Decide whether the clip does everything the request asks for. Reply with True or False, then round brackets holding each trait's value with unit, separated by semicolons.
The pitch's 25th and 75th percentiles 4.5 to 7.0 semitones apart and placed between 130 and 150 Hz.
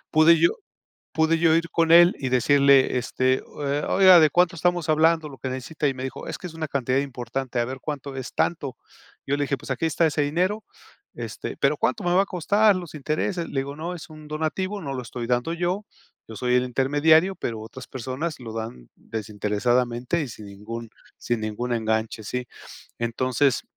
True (5.0 semitones; 140 Hz)